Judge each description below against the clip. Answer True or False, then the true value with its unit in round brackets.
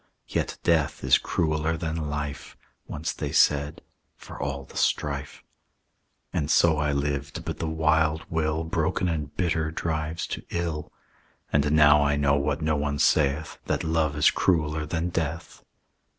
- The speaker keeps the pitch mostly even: True (1.8 semitones)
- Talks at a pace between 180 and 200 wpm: False (150 wpm)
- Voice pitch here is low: True (75 Hz)